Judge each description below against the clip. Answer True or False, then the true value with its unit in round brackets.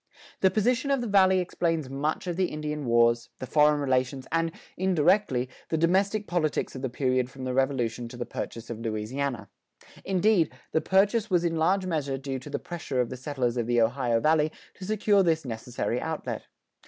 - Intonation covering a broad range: True (6.1 semitones)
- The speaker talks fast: False (190 wpm)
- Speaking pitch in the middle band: True (150 Hz)